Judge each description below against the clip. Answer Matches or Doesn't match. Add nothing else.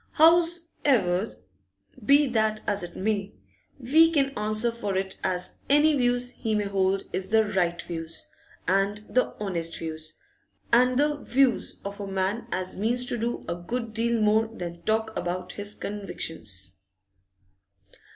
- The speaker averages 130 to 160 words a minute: Matches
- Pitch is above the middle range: Matches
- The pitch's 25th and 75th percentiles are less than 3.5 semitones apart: Doesn't match